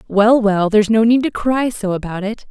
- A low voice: No, high, 215 Hz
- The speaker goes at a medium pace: No, fast, 240 wpm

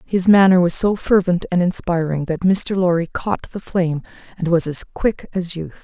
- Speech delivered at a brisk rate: No, average, 195 wpm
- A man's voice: No, female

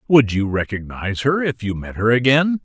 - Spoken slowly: No, fast, 205 wpm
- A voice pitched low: Yes, low, 120 Hz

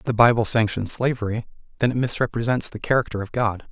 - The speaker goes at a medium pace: Yes, average, 195 wpm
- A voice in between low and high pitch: No, low, 115 Hz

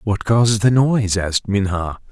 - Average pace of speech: Yes, average, 170 wpm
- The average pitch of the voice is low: Yes, low, 105 Hz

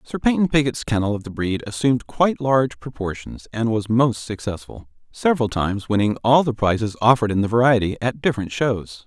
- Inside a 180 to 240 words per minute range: Yes, average, 185 wpm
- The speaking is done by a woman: No, male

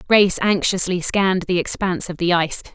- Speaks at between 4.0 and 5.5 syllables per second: No, 6.2 syllables/s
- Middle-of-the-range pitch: Yes, medium, 180 Hz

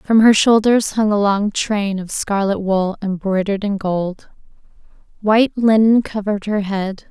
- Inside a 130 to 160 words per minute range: Yes, average, 150 wpm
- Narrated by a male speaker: No, female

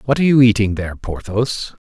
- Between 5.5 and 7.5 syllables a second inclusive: Yes, 6.0 syllables/s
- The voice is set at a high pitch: No, low, 115 Hz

